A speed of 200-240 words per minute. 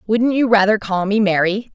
Yes: fast, 205 wpm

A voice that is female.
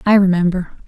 Yes: female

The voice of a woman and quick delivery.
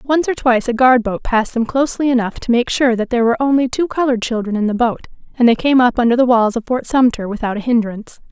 Yes: female; fast, 260 wpm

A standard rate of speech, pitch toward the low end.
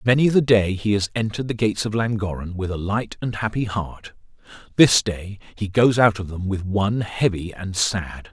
Yes: average, 195 wpm; low, 100 Hz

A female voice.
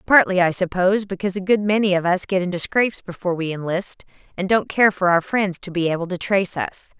Yes: female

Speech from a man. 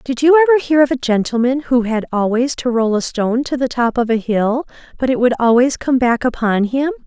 No: female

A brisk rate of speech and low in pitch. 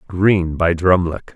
No: slow, 135 wpm; very low, 90 Hz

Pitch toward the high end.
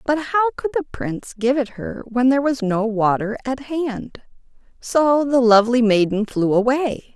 Yes: very high, 250 Hz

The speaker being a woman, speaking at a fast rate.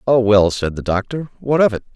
No: male; fast, 245 wpm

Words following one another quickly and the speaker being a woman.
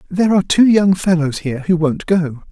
No: fast, 215 wpm; male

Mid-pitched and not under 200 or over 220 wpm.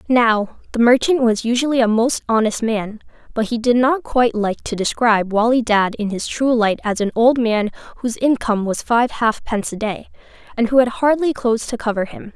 No: high, 230 Hz; fast, 205 wpm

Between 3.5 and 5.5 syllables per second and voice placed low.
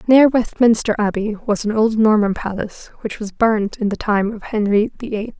No: 4.9 syllables/s; high, 215 Hz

